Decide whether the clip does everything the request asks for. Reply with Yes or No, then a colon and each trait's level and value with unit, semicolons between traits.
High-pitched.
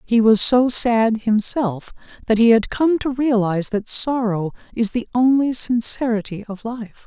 Yes: high, 230 Hz